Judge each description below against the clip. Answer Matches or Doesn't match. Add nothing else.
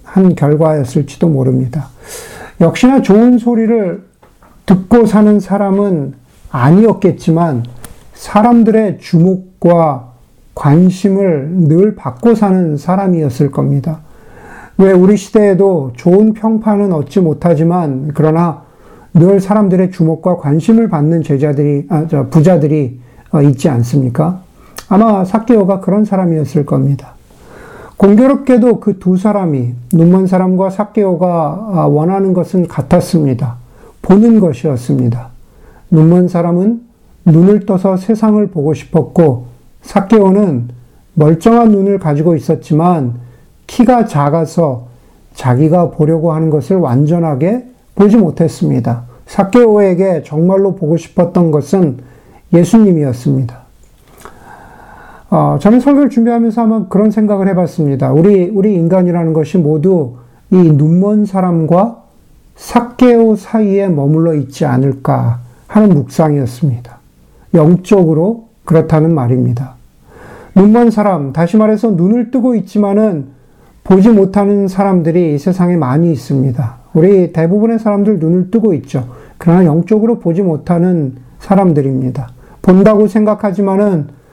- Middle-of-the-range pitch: Matches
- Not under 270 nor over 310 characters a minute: Matches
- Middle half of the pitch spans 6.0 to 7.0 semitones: Doesn't match